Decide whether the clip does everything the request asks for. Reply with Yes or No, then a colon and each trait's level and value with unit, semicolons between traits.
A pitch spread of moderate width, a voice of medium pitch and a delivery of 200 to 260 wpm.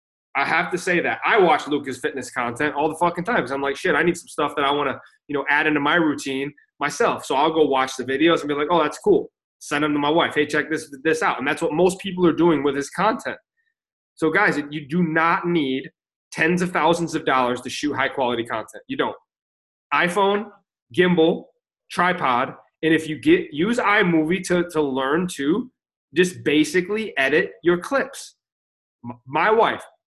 Yes: average, 3.8 semitones; medium, 155 Hz; fast, 205 wpm